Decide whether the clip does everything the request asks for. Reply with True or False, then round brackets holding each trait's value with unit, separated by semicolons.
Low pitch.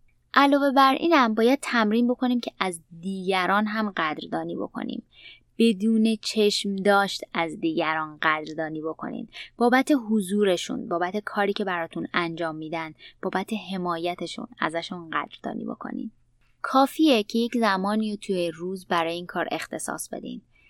False (200 Hz)